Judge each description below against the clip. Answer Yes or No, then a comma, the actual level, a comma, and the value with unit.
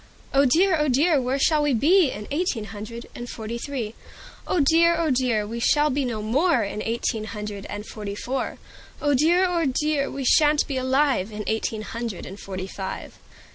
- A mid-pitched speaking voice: No, very high, 255 Hz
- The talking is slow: No, average, 190 wpm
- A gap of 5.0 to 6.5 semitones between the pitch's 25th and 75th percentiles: Yes, wide, 5.6 semitones